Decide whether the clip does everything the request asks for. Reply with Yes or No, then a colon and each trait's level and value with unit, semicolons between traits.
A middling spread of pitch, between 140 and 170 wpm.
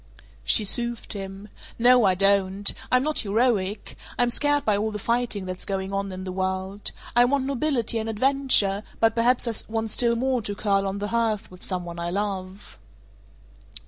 No: average, 3.6 semitones; average, 180 wpm